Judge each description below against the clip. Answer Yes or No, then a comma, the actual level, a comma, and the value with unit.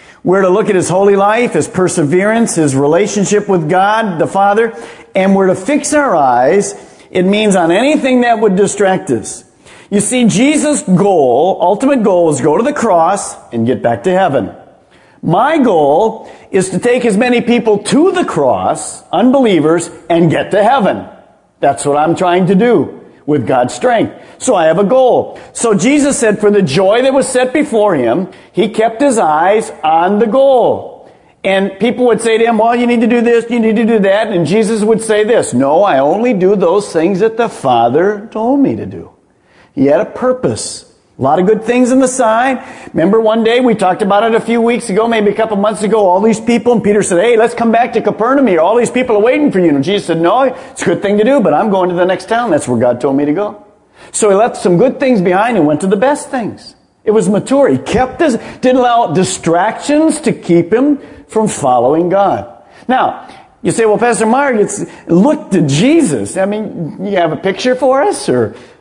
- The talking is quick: Yes, fast, 215 wpm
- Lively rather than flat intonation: No, average, 4.5 semitones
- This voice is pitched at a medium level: No, high, 215 Hz